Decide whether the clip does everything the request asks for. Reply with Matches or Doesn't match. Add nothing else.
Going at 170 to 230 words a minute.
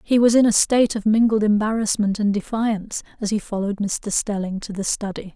Matches